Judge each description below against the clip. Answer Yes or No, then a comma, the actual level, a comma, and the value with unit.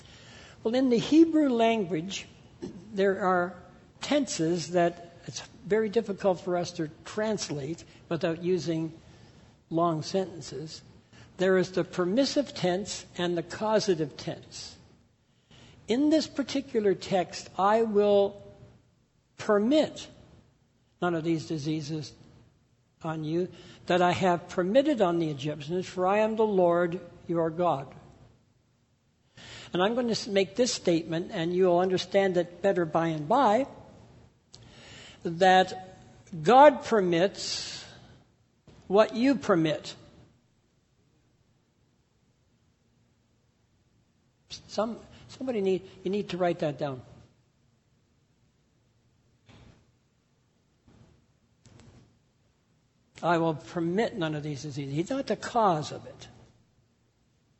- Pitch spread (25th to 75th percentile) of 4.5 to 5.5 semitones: Yes, average, 4.8 semitones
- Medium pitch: Yes, medium, 175 Hz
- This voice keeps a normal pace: No, slow, 105 wpm